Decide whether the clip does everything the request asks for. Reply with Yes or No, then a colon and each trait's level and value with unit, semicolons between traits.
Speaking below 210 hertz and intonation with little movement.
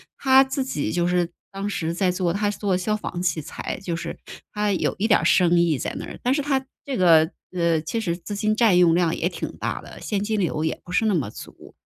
No: medium, 185 Hz; average, 3.9 semitones